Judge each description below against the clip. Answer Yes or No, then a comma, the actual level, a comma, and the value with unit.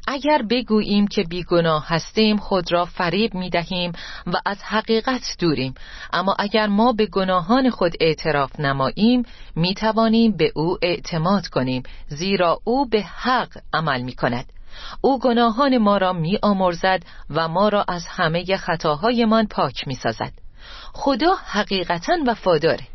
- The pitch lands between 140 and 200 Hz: Yes, medium, 185 Hz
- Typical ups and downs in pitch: Yes, average, 4.9 semitones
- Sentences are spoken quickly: No, average, 140 wpm